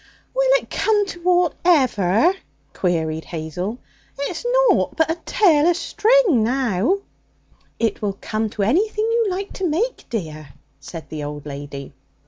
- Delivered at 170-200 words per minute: No, average, 145 wpm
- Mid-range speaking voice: No, very high, 255 Hz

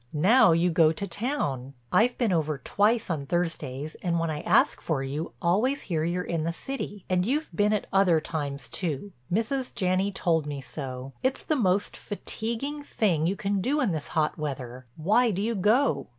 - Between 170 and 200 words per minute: Yes, average, 185 wpm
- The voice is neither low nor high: Yes, medium, 180 Hz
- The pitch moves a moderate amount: No, wide, 5.9 semitones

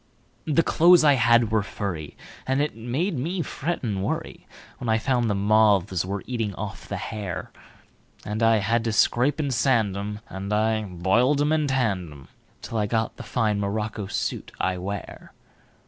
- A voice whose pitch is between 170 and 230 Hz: No, low, 110 Hz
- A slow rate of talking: No, average, 165 wpm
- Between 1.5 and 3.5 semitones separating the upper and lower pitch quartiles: No, average, 4.2 semitones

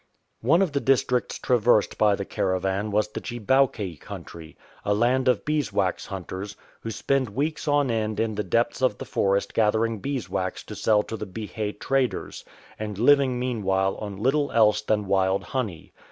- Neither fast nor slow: Yes, average, 170 wpm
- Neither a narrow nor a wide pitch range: Yes, average, 4.3 semitones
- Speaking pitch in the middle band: No, low, 110 Hz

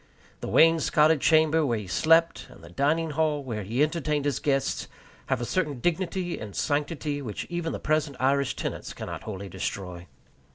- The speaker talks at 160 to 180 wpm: Yes, average, 170 wpm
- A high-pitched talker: No, medium, 145 Hz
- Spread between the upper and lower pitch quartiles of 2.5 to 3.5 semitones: No, average, 4.2 semitones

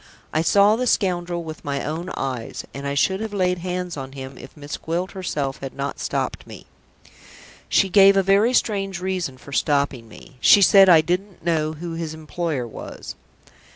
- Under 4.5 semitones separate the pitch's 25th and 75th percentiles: No, average, 5.1 semitones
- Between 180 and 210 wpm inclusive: Yes, average, 185 wpm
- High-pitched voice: No, medium, 170 Hz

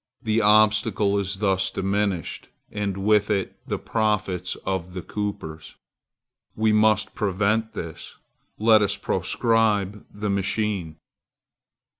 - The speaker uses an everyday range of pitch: No, narrow, 2.0 semitones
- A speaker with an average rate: No, slow, 110 wpm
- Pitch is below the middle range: Yes, low, 105 Hz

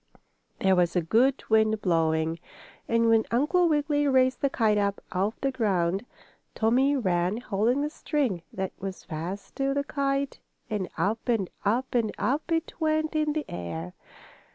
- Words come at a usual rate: Yes, average, 160 wpm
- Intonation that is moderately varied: No, wide, 6.4 semitones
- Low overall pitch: No, high, 225 Hz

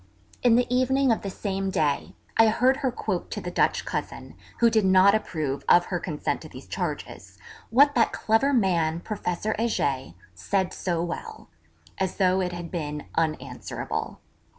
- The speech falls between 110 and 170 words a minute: Yes, average, 165 wpm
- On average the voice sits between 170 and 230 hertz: Yes, high, 190 Hz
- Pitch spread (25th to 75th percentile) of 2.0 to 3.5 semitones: No, average, 5.3 semitones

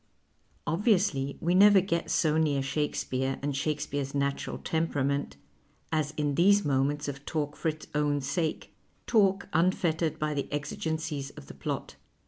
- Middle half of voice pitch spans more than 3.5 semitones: No, average, 2.9 semitones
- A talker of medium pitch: Yes, medium, 150 Hz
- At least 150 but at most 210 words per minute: No, average, 140 wpm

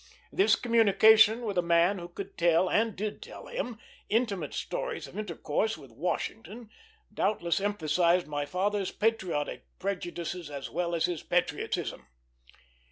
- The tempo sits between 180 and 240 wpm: No, slow, 135 wpm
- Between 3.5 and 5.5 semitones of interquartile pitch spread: Yes, average, 4.4 semitones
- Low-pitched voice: No, high, 190 Hz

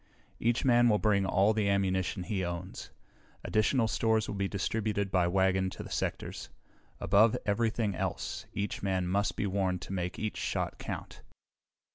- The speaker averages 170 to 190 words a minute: No, average, 160 wpm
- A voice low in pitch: Yes, low, 100 Hz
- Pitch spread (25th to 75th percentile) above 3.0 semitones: No, narrow, 2.5 semitones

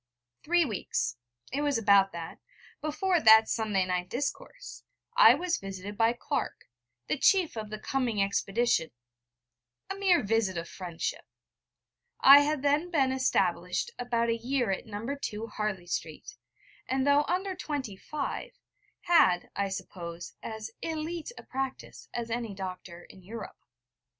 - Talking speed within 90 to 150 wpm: Yes, average, 140 wpm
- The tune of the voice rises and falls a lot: Yes, wide, 6.7 semitones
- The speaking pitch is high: Yes, high, 230 Hz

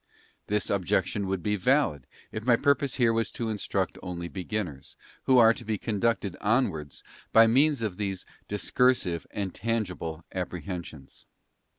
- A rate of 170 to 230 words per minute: No, average, 150 wpm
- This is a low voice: Yes, low, 105 Hz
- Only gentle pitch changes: No, average, 4.2 semitones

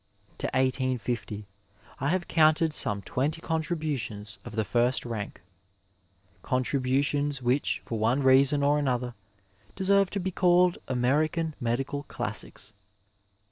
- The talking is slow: Yes, slow, 120 wpm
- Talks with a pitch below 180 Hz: Yes, low, 135 Hz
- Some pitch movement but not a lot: Yes, average, 4.3 semitones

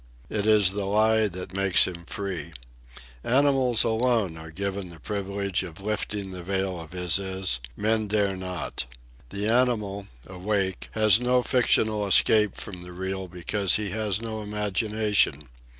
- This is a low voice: Yes, low, 100 Hz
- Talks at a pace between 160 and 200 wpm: No, average, 145 wpm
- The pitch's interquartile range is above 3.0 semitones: No, average, 2.7 semitones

